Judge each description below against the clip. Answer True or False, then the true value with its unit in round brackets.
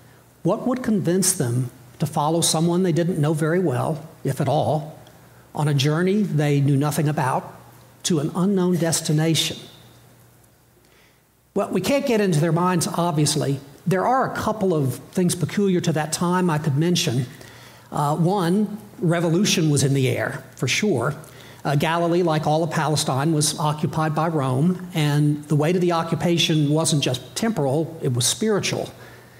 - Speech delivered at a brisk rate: False (160 wpm)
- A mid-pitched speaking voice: True (160 Hz)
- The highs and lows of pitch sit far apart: False (3.0 semitones)